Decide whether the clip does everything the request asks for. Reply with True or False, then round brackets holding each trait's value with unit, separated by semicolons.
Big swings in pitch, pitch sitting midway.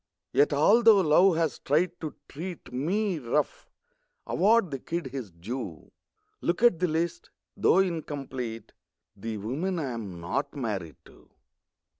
True (7.0 semitones; 150 Hz)